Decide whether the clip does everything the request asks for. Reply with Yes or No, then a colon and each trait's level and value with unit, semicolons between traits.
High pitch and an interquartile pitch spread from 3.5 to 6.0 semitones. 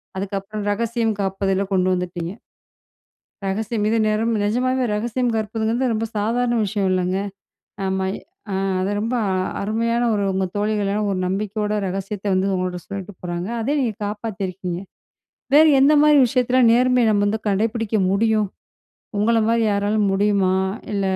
No: high, 210 Hz; average, 3.0 semitones